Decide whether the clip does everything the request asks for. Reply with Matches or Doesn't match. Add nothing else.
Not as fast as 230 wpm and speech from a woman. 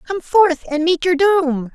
Matches